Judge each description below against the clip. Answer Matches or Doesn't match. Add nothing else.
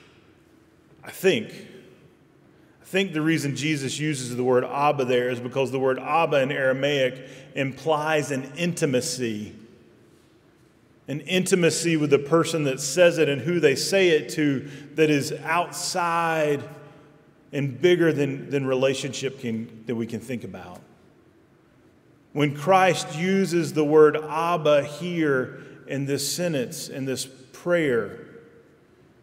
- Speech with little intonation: Doesn't match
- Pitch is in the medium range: Matches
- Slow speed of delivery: Matches